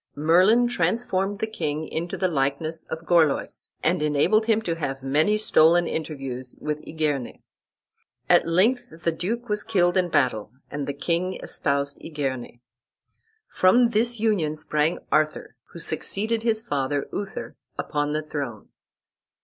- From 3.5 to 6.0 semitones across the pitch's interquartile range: Yes, average, 5.3 semitones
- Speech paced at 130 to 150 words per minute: Yes, average, 140 wpm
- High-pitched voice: No, medium, 165 Hz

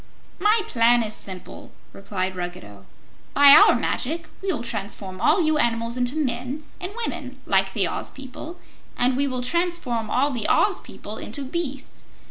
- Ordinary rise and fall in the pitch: No, wide, 6.0 semitones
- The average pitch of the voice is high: Yes, very high, 250 Hz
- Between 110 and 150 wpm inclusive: No, average, 160 wpm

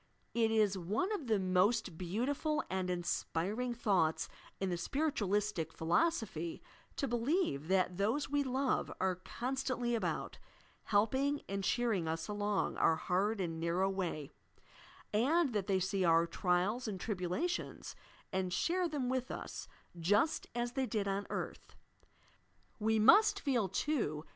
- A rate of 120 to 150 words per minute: Yes, average, 140 wpm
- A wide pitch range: Yes, wide, 5.7 semitones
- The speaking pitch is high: Yes, high, 210 Hz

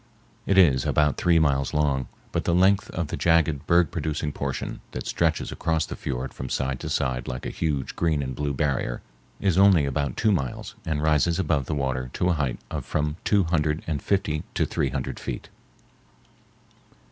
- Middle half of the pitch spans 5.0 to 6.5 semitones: No, average, 3.7 semitones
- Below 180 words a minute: No, average, 190 wpm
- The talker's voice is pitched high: No, very low, 75 Hz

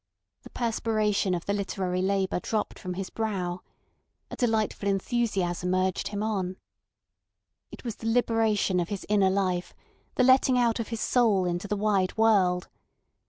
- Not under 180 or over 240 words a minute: No, average, 155 wpm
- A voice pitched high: Yes, high, 200 Hz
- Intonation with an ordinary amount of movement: Yes, average, 3.2 semitones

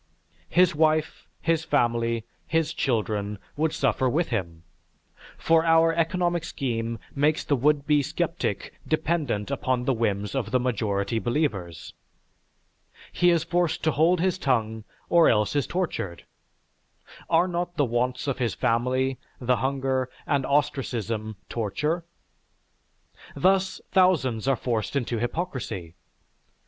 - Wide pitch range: Yes, wide, 6.0 semitones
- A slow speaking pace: Yes, slow, 125 wpm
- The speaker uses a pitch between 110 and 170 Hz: Yes, low, 135 Hz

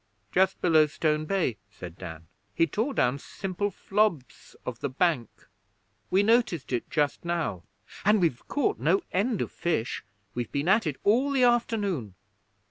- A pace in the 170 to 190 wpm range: No, average, 155 wpm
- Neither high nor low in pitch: Yes, medium, 170 Hz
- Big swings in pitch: Yes, wide, 8.0 semitones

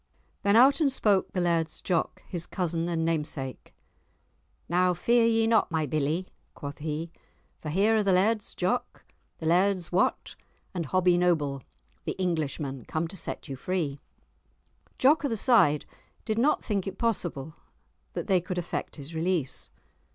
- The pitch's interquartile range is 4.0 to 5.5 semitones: Yes, average, 4.3 semitones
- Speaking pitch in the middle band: Yes, medium, 175 Hz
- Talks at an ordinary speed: Yes, average, 160 wpm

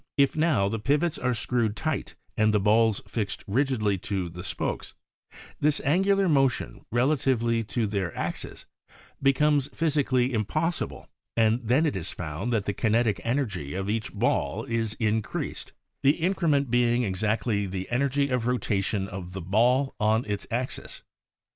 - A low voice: Yes, low, 115 Hz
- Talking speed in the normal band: Yes, average, 155 wpm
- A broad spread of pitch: No, average, 4.9 semitones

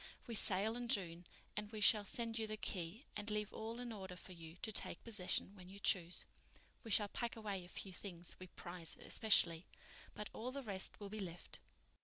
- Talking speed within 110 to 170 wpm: No, fast, 205 wpm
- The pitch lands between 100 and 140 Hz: No, high, 205 Hz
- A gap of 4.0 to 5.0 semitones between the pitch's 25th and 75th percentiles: No, average, 3.4 semitones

